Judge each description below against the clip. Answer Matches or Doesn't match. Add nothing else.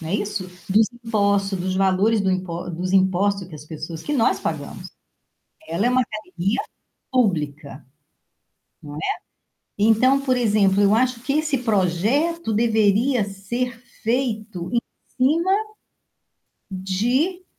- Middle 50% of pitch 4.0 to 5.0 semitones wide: Matches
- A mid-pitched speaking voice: Doesn't match